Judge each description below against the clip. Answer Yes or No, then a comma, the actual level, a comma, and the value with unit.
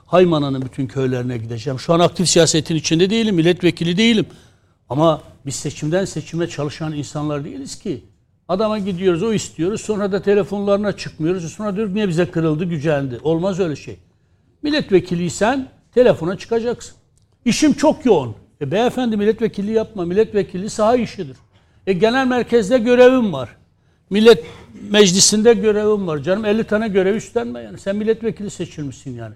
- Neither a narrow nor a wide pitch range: No, wide, 6.3 semitones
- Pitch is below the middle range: No, medium, 185 Hz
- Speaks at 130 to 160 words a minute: Yes, fast, 140 wpm